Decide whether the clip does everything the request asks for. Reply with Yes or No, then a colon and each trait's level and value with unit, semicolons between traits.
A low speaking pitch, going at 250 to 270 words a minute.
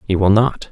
Yes: low, 105 Hz; fast, 255 wpm